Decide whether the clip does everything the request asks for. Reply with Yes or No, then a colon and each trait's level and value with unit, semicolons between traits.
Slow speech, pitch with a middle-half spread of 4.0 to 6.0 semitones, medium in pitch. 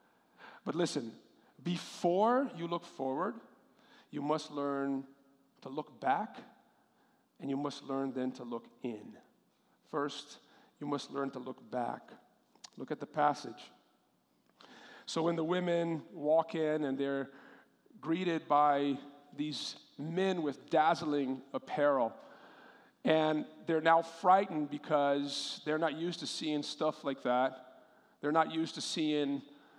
No: slow, 130 wpm; average, 2.9 semitones; medium, 150 Hz